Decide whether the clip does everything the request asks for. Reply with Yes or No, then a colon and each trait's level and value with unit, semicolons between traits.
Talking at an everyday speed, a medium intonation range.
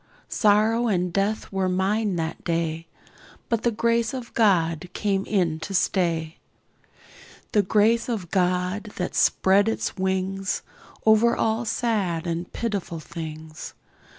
No: slow, 125 wpm; average, 4.1 semitones